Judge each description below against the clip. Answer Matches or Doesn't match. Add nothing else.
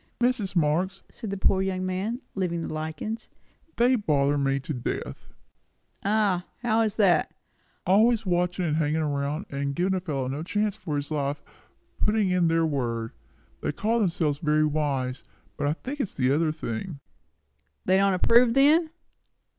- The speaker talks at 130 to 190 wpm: Matches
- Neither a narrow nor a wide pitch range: Doesn't match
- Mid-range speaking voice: Matches